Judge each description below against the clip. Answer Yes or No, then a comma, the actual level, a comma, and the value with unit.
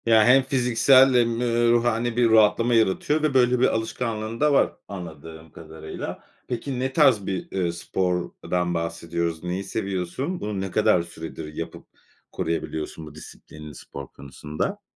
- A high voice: No, low, 105 Hz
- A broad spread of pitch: Yes, wide, 6.4 semitones